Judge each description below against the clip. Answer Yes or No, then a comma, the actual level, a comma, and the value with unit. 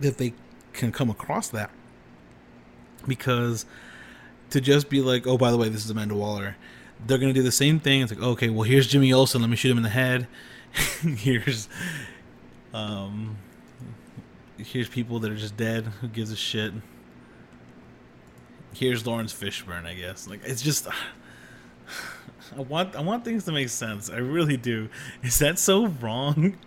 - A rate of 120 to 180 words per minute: Yes, average, 165 wpm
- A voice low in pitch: Yes, low, 115 Hz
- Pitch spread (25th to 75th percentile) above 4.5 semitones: Yes, average, 5.2 semitones